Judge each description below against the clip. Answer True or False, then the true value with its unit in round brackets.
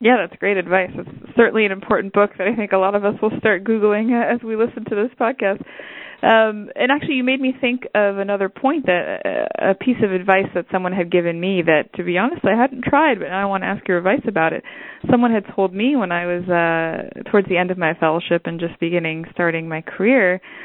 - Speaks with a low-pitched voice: False (200 Hz)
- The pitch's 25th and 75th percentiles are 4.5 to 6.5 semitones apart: True (4.9 semitones)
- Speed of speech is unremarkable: False (240 wpm)